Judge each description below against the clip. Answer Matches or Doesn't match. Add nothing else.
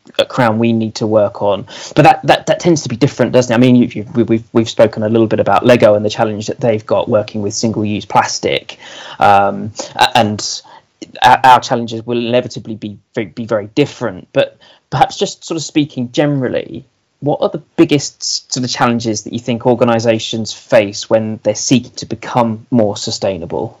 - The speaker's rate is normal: Matches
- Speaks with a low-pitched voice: Matches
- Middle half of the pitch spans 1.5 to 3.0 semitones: Matches